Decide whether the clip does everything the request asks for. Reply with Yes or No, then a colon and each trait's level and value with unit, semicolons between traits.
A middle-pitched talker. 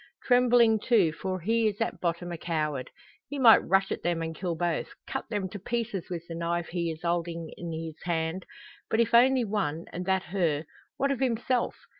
Yes: medium, 180 Hz